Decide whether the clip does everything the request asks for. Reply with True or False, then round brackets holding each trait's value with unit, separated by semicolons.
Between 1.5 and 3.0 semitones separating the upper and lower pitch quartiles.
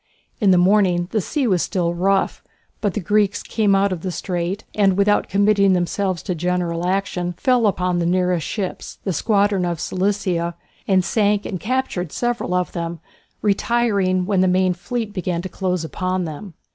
True (2.4 semitones)